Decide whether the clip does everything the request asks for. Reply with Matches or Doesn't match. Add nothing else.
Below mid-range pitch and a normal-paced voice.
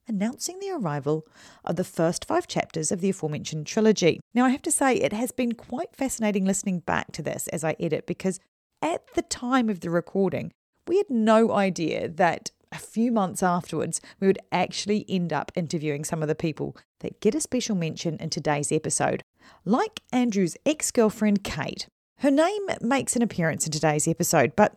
Doesn't match